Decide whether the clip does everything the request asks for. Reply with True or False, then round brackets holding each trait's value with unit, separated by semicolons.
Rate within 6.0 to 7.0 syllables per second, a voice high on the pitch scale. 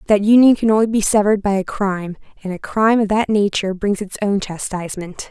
True (6.2 syllables/s; 205 Hz)